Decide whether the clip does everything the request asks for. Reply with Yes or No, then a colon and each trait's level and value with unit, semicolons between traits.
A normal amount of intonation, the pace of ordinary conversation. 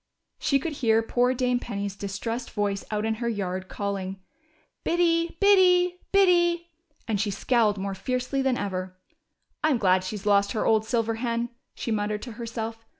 Yes: average, 4.3 semitones; average, 160 wpm